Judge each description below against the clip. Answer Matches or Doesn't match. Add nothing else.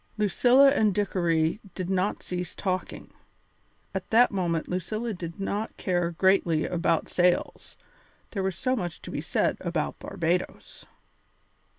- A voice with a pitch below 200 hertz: Matches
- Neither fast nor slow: Doesn't match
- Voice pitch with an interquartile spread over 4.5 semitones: Doesn't match